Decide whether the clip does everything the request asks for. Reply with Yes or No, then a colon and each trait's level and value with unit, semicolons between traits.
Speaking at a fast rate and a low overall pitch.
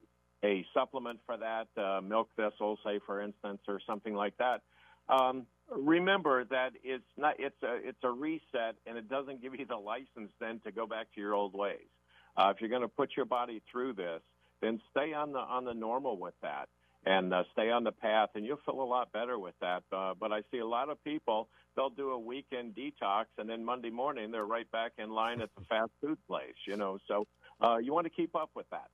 Yes: fast, 220 wpm; low, 115 Hz